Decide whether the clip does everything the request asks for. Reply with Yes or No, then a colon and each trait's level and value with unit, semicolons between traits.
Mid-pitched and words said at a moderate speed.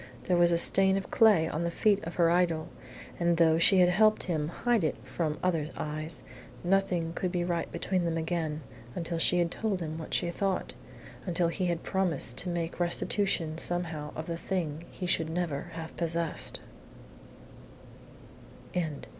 Yes: medium, 170 Hz; average, 170 wpm